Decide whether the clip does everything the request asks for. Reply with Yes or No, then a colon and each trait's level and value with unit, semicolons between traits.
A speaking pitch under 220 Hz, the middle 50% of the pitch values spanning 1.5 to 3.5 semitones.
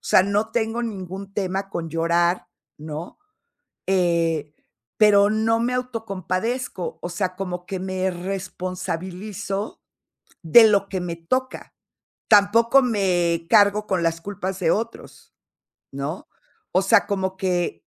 Yes: high, 190 Hz; average, 3.2 semitones